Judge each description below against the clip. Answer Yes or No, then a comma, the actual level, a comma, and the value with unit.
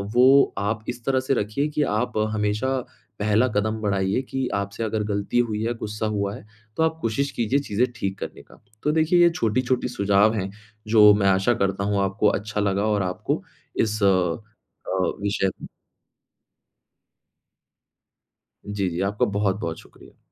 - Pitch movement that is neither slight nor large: Yes, average, 3.3 semitones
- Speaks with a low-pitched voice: Yes, low, 105 Hz